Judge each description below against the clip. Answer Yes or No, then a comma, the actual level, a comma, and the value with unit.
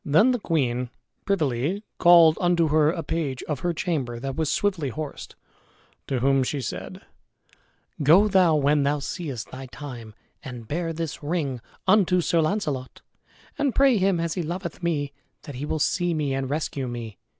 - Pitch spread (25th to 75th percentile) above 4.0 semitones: Yes, average, 4.4 semitones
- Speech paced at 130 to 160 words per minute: No, average, 170 wpm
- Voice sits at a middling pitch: Yes, medium, 155 Hz